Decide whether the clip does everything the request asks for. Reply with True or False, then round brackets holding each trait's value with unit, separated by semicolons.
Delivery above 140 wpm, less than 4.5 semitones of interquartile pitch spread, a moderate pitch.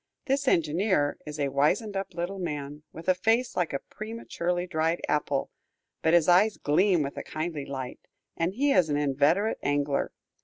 False (175 wpm; 4.8 semitones; 170 Hz)